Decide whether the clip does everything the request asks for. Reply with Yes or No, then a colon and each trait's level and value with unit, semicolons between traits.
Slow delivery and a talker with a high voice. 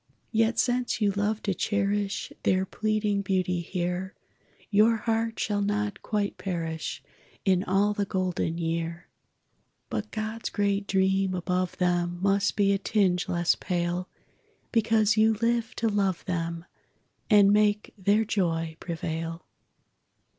Yes: slow, 130 wpm; high, 200 Hz